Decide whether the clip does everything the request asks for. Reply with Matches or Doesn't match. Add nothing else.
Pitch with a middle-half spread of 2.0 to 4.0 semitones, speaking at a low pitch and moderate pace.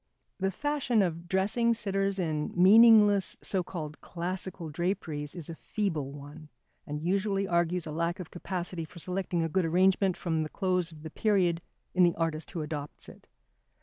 Doesn't match